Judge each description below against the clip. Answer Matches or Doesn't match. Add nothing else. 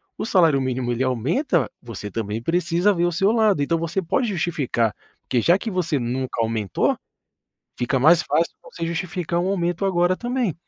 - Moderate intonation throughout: Doesn't match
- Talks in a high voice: Doesn't match